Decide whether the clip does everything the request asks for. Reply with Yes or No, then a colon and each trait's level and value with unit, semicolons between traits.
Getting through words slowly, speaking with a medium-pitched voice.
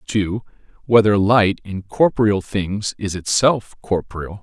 No: slow, 120 wpm; low, 100 Hz